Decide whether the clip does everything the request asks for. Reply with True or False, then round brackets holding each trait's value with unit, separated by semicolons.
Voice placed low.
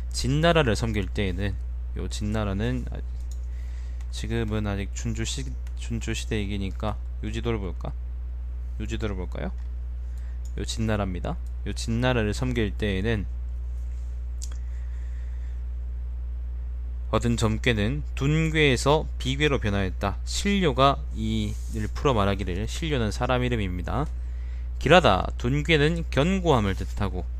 True (95 Hz)